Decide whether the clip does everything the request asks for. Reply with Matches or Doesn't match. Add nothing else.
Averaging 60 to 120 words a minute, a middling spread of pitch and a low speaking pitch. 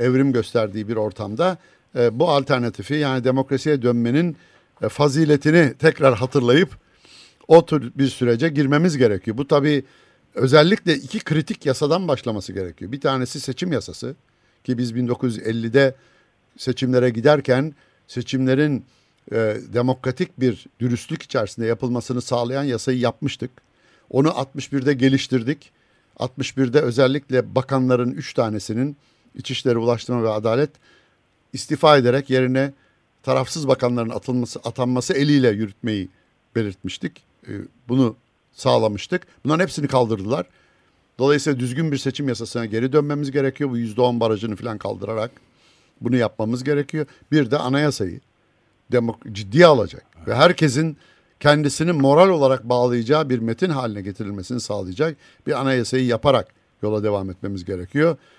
Matches